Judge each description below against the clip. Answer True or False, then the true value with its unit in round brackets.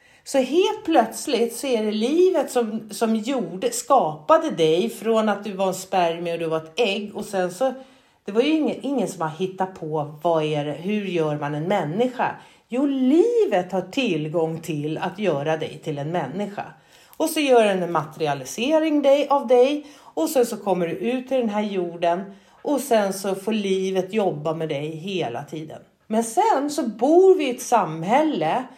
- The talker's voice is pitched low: False (210 Hz)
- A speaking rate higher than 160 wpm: True (185 wpm)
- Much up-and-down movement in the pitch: True (7.1 semitones)